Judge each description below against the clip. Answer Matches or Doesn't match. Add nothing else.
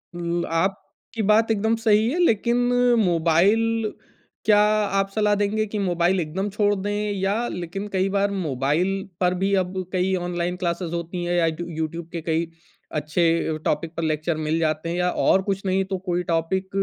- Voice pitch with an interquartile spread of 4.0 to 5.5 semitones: Doesn't match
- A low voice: Doesn't match